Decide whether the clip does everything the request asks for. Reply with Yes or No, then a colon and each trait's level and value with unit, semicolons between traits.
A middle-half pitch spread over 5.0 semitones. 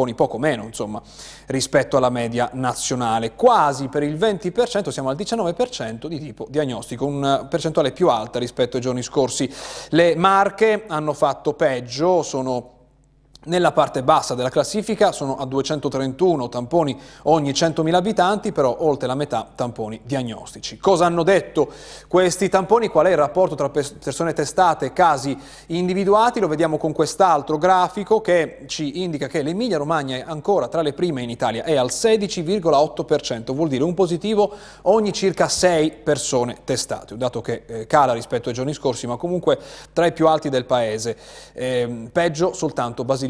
Yes: wide, 5.5 semitones